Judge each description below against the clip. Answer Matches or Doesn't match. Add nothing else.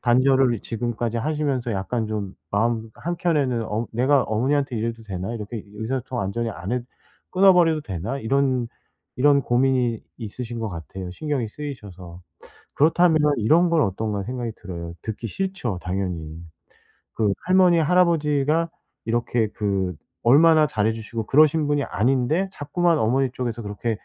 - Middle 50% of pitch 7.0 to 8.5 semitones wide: Doesn't match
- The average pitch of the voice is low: Matches